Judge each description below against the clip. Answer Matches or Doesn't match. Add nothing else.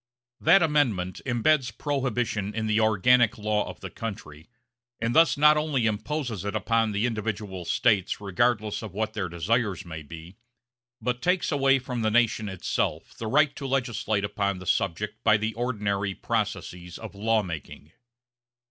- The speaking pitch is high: Doesn't match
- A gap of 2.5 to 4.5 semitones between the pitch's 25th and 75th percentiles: Matches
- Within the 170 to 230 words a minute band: Doesn't match